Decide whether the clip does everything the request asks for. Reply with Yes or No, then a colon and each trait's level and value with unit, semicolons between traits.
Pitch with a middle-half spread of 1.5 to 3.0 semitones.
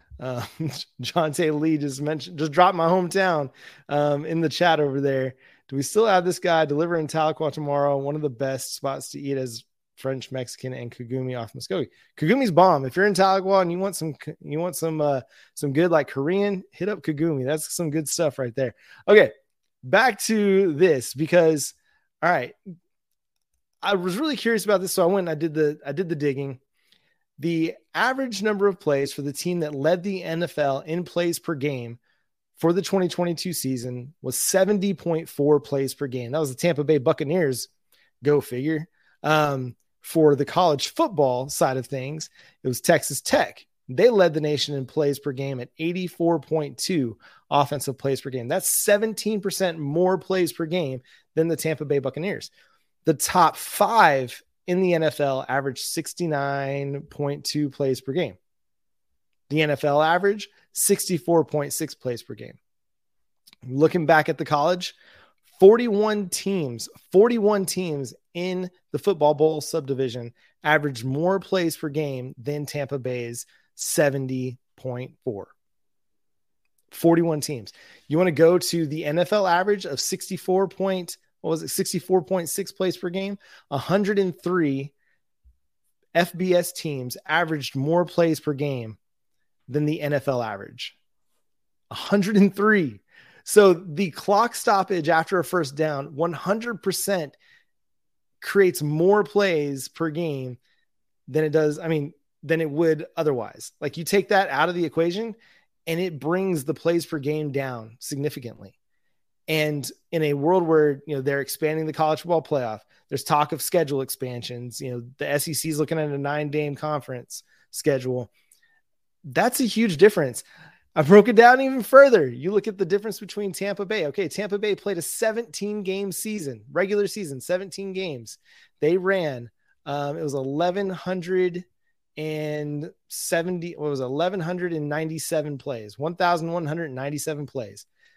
No: average, 4.6 semitones